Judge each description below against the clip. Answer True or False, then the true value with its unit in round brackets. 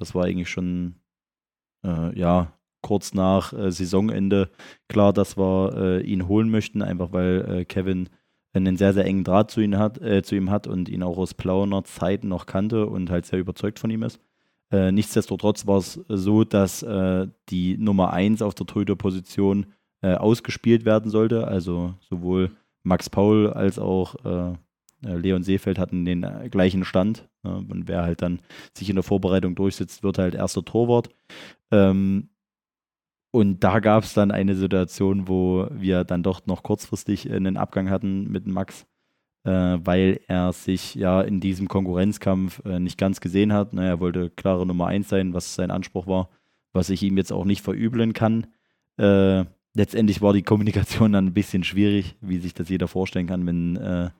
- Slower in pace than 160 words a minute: False (170 wpm)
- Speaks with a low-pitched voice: True (95 Hz)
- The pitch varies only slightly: True (2.0 semitones)